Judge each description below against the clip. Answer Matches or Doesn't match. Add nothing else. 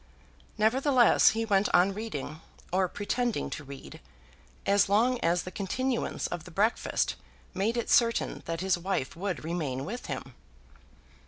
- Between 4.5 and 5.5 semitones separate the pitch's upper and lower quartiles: Matches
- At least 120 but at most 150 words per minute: Matches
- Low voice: Doesn't match